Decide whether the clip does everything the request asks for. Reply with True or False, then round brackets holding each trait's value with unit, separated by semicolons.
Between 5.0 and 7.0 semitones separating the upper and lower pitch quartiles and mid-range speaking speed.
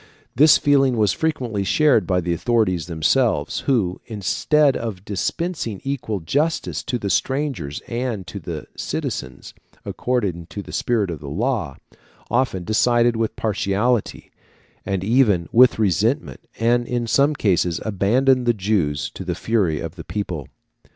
True (5.5 semitones; 145 wpm)